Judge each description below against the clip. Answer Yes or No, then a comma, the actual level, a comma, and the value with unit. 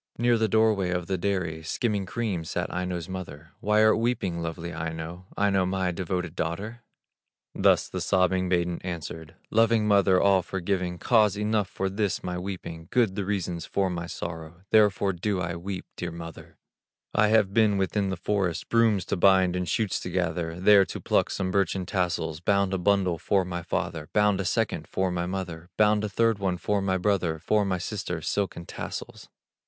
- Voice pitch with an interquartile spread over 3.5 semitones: No, average, 2.8 semitones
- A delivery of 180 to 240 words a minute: Yes, average, 185 wpm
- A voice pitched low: Yes, very low, 95 Hz